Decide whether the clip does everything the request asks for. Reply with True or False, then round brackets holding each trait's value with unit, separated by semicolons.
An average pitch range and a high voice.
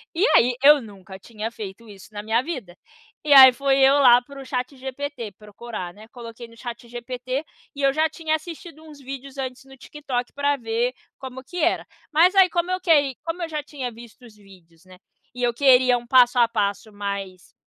True (4.0 semitones; 250 Hz)